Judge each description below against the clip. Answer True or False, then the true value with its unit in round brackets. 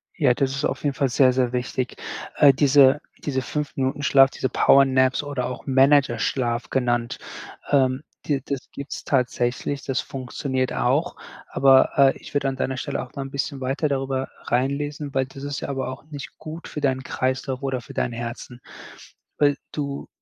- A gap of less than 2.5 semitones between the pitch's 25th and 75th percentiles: True (1.6 semitones)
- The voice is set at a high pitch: False (135 Hz)